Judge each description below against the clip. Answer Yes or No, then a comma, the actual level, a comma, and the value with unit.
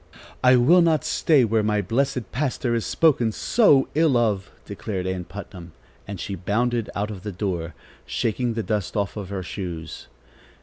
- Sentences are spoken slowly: No, average, 165 wpm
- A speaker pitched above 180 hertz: No, low, 105 Hz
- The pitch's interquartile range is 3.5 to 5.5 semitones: Yes, average, 4.5 semitones